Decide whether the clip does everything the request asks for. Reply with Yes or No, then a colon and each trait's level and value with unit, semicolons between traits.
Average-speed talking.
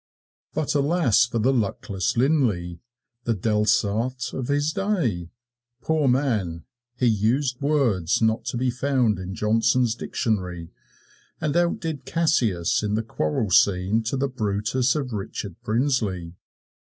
No: slow, 130 wpm